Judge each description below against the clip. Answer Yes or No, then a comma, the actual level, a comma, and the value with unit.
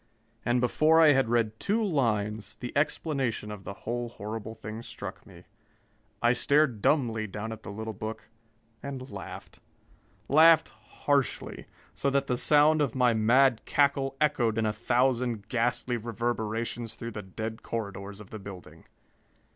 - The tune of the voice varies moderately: Yes, average, 3.9 semitones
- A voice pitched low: Yes, low, 120 Hz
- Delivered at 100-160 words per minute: Yes, average, 150 wpm